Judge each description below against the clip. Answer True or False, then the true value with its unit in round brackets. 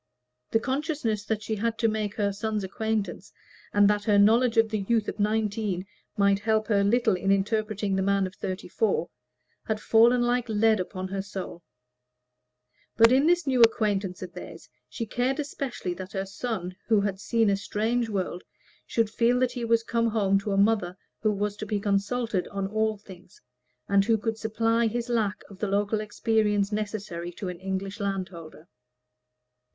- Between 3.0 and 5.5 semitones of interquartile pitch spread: False (2.4 semitones)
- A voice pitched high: True (210 Hz)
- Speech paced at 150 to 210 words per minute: True (180 wpm)